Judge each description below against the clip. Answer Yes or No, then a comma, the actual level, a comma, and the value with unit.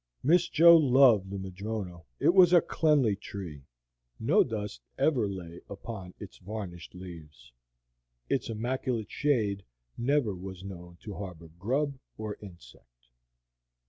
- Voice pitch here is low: Yes, low, 100 Hz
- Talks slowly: Yes, slow, 125 wpm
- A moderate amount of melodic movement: No, wide, 6.1 semitones